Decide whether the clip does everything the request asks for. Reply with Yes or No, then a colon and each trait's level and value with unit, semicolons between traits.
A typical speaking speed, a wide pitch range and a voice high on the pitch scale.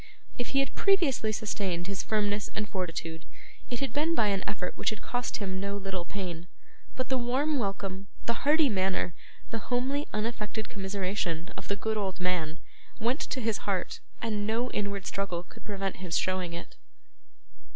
No: average, 170 wpm; average, 4.0 semitones; high, 205 Hz